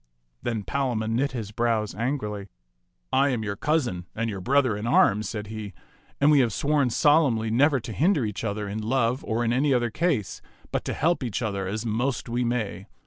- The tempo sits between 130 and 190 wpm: No, average, 200 wpm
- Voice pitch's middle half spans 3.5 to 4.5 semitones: Yes, average, 4.0 semitones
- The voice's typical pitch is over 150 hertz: No, low, 115 Hz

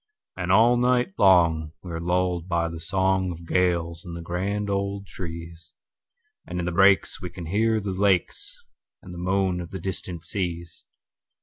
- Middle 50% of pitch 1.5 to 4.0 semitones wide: Yes, narrow, 2.5 semitones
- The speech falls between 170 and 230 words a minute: No, average, 160 wpm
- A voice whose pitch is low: Yes, very low, 90 Hz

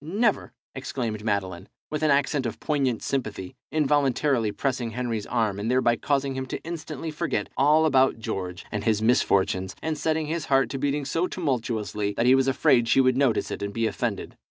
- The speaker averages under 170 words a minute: No, average, 185 wpm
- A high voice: No, low, 130 Hz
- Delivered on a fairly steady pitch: No, average, 4.8 semitones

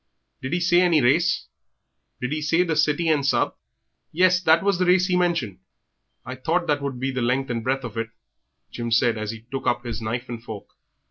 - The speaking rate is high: Yes, fast, 225 wpm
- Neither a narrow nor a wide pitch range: No, wide, 6.1 semitones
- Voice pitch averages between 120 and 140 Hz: Yes, low, 135 Hz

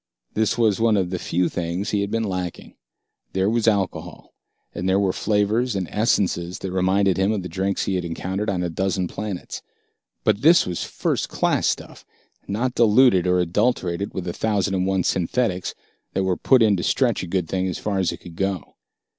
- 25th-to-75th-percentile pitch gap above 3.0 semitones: No, average, 2.7 semitones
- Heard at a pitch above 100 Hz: No, very low, 95 Hz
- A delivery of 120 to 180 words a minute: No, average, 200 wpm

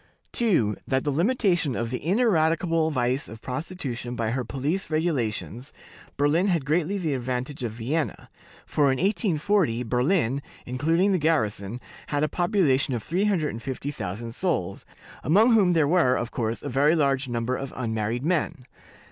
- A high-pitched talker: No, medium, 145 Hz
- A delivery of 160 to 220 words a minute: No, average, 150 wpm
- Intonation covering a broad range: Yes, wide, 5.7 semitones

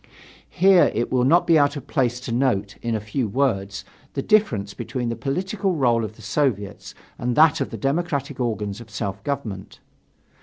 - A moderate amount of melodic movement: Yes, average, 4.9 semitones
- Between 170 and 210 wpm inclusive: Yes, average, 185 wpm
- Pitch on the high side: No, low, 125 Hz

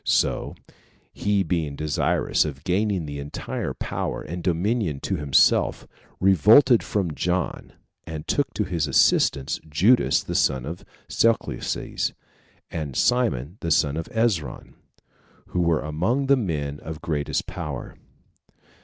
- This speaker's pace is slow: Yes, slow, 125 wpm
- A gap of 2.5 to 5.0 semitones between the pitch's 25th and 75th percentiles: No, wide, 5.5 semitones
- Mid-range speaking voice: No, very low, 85 Hz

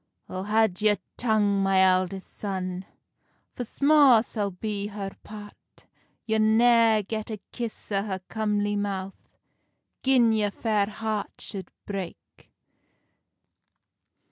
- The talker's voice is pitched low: No, high, 210 Hz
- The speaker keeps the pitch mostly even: Yes, narrow, 2.1 semitones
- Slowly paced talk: Yes, slow, 120 wpm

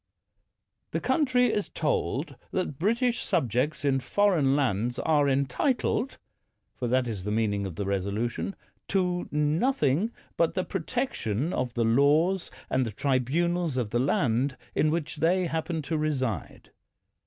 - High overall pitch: No, medium, 145 Hz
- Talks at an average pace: Yes, average, 155 wpm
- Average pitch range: No, wide, 6.5 semitones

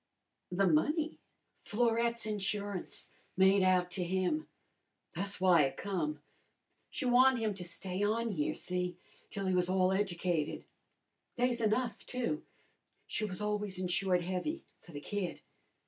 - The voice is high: Yes, high, 195 Hz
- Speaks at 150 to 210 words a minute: No, slow, 135 wpm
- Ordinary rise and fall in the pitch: Yes, average, 3.5 semitones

